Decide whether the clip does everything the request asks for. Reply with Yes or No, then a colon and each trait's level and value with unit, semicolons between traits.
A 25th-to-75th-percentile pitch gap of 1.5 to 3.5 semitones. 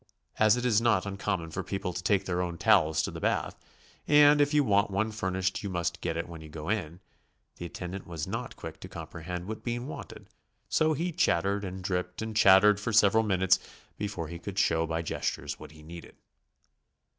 No: average, 3.9 semitones